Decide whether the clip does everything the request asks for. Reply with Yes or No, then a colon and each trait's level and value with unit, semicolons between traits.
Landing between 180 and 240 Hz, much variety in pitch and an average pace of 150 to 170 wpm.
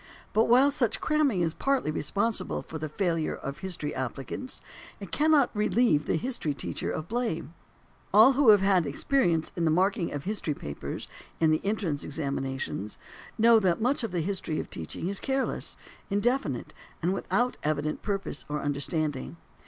Yes: medium, 185 Hz; wide, 7.2 semitones; average, 160 wpm